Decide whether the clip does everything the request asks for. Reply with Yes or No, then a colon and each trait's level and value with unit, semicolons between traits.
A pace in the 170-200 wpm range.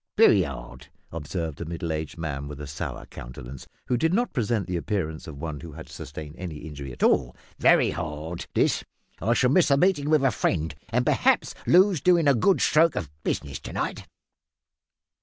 Yes: average, 185 wpm